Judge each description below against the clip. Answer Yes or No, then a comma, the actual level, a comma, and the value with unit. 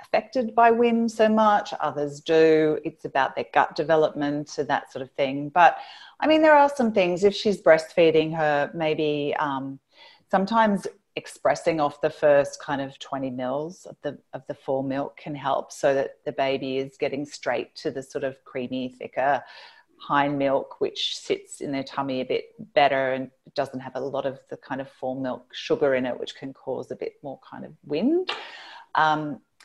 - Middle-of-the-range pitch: Yes, medium, 150 Hz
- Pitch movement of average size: No, wide, 7.0 semitones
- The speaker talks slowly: No, average, 190 wpm